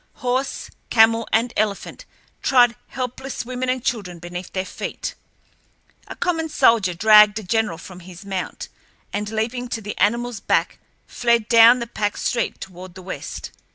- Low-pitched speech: No, high, 220 Hz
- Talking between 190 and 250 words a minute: No, average, 155 wpm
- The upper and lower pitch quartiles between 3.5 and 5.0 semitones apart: Yes, average, 3.9 semitones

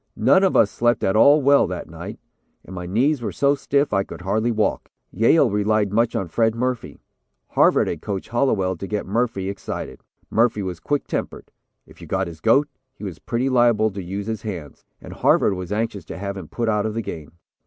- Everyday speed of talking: No, fast, 210 wpm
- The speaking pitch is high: No, low, 110 Hz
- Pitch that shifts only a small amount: No, average, 3.7 semitones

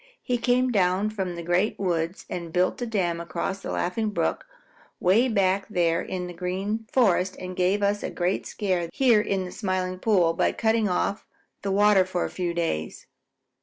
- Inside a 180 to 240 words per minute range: Yes, average, 185 wpm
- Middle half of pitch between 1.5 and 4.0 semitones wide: Yes, average, 2.8 semitones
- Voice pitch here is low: No, medium, 185 Hz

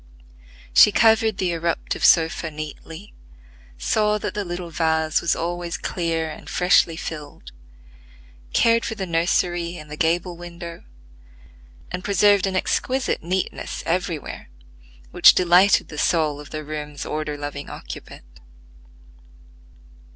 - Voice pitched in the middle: Yes, medium, 170 Hz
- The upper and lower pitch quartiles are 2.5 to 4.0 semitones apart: Yes, average, 3.0 semitones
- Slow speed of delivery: Yes, slow, 120 wpm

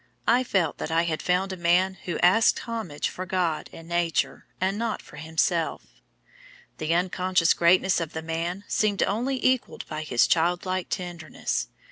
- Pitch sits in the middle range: Yes, medium, 175 Hz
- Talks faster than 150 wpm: Yes, average, 165 wpm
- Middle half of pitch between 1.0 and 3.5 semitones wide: Yes, narrow, 2.5 semitones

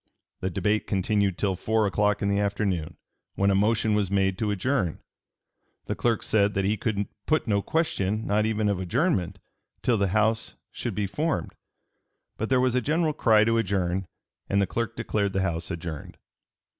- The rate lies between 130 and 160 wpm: No, average, 180 wpm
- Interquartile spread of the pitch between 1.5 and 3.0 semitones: Yes, narrow, 2.5 semitones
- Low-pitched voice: Yes, low, 105 Hz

